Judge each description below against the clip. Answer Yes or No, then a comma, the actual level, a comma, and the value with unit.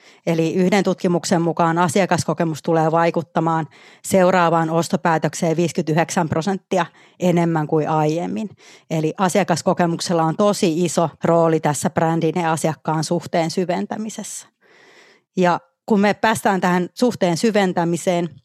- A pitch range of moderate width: No, narrow, 2.3 semitones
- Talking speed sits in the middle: Yes, average, 105 wpm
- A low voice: No, medium, 170 Hz